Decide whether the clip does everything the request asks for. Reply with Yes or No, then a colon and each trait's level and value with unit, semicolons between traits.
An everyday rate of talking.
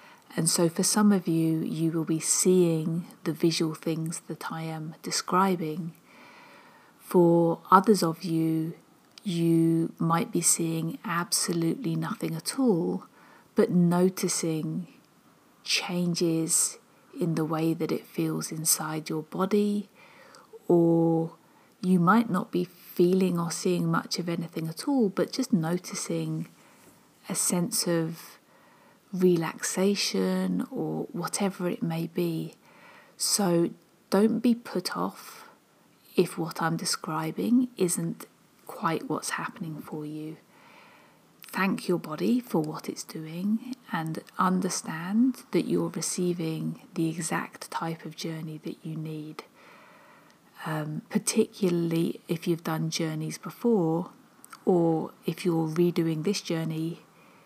No: slow, 120 wpm